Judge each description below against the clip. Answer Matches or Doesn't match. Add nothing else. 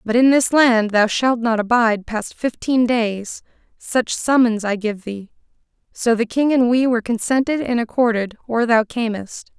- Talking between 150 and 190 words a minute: Matches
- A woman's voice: Matches